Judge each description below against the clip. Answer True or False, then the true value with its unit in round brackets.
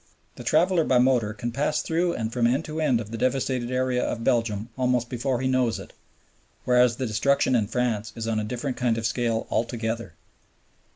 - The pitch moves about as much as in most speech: False (2.3 semitones)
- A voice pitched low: True (125 Hz)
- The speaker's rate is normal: True (195 wpm)